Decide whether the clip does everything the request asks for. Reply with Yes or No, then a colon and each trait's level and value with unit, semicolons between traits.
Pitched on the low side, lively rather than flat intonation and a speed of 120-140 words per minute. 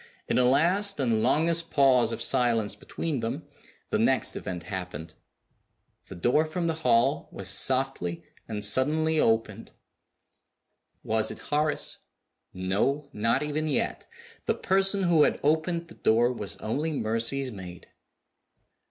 Yes: low, 130 Hz; wide, 6.0 semitones; slow, 135 wpm